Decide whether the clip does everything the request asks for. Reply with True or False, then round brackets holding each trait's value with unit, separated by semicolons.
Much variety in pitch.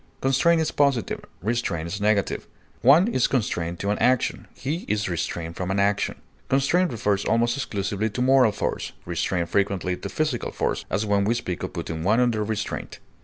False (4.8 semitones)